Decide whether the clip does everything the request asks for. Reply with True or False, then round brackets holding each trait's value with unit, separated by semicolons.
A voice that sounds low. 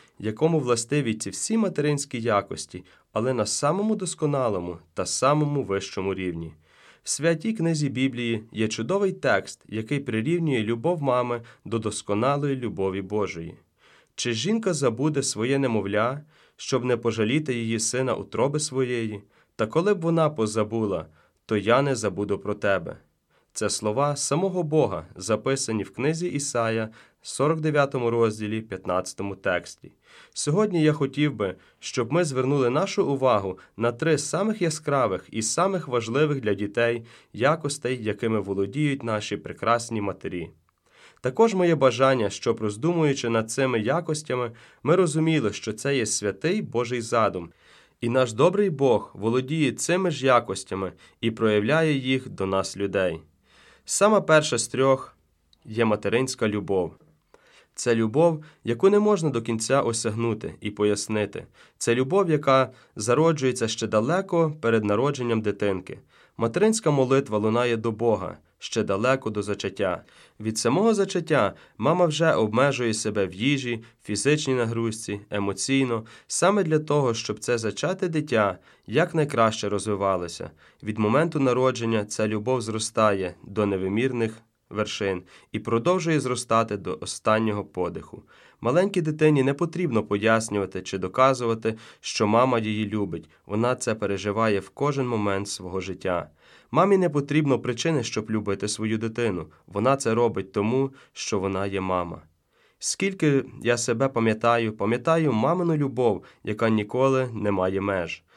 True (120 Hz)